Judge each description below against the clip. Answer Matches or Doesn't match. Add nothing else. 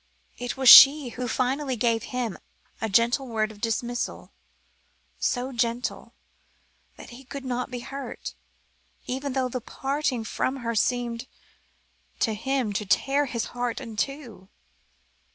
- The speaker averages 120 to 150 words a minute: Matches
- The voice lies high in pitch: Matches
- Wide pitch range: Doesn't match